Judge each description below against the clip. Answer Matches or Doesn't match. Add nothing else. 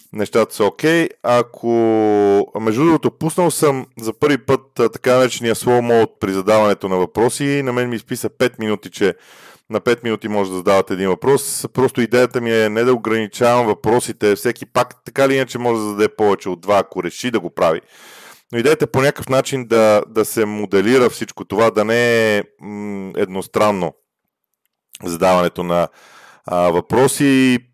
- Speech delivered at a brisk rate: Matches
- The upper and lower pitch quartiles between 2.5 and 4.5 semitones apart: Matches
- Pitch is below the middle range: Matches